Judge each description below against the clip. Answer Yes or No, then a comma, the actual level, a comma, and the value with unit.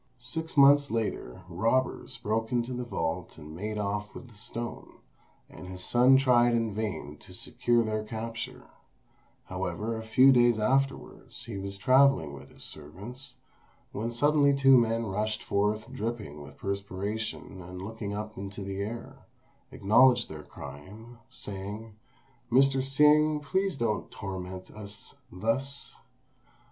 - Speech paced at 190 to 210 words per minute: No, slow, 135 wpm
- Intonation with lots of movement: No, average, 4.0 semitones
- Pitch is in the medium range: No, low, 110 Hz